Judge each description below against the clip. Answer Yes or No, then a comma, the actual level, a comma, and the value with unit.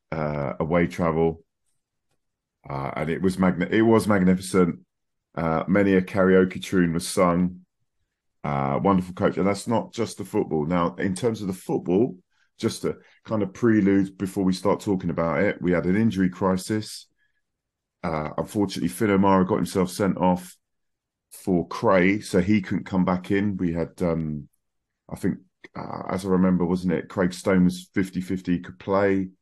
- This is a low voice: Yes, very low, 95 Hz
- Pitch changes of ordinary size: No, narrow, 2.1 semitones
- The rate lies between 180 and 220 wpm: No, average, 170 wpm